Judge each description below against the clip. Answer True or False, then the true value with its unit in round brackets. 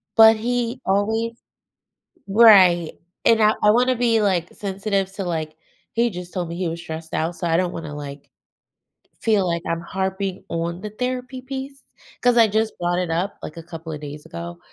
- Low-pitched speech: False (190 Hz)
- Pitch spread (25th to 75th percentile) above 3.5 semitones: True (5.0 semitones)